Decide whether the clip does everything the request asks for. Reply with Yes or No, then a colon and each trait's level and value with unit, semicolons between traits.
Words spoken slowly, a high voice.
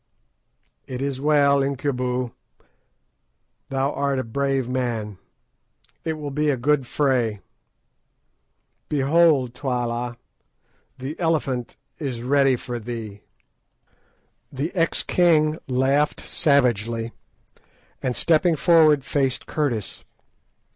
No: slow, 95 wpm; low, 135 Hz